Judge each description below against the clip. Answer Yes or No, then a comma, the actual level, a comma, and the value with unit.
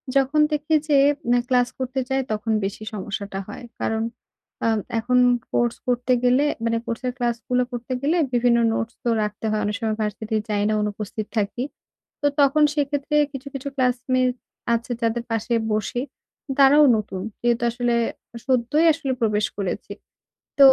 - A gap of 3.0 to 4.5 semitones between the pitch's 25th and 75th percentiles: Yes, average, 3.3 semitones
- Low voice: No, high, 240 Hz